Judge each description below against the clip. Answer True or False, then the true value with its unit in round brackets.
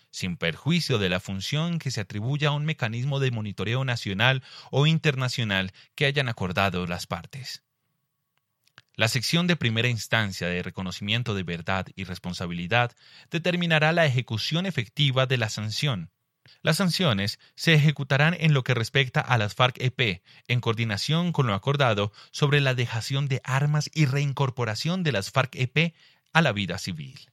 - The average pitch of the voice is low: True (130 Hz)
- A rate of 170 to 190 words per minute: False (150 wpm)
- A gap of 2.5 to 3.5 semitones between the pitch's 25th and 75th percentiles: False (5.5 semitones)